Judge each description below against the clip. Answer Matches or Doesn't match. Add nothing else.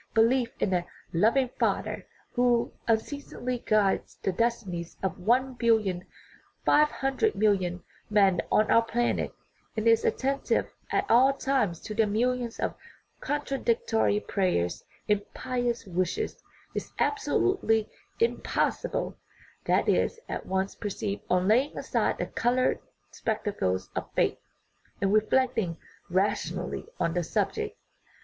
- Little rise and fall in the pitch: Doesn't match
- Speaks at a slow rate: Matches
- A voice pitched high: Matches